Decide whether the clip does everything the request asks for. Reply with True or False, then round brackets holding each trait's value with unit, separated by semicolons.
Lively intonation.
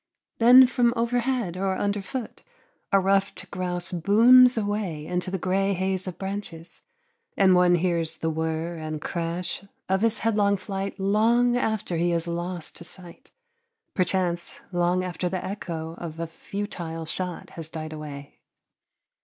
False (3.2 semitones)